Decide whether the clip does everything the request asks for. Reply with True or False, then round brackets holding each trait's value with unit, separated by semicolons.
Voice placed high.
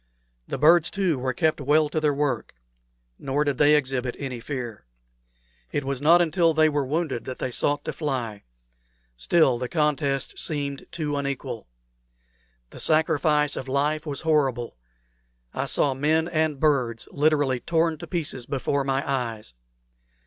False (145 Hz)